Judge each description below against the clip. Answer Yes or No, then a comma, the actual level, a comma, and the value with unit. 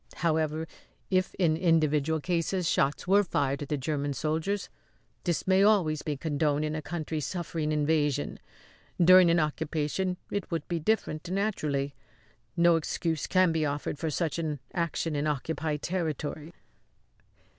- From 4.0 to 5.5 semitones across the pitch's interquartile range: No, narrow, 2.5 semitones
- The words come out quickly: No, average, 145 wpm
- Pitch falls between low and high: Yes, medium, 160 Hz